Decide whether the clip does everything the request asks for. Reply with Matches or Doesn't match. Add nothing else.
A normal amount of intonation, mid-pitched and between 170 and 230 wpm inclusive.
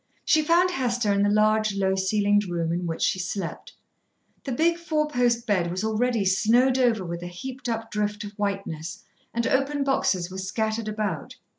Doesn't match